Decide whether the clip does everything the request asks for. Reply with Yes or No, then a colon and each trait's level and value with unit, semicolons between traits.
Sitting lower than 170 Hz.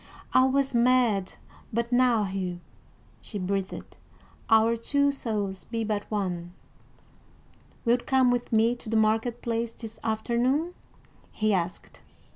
No: high, 225 Hz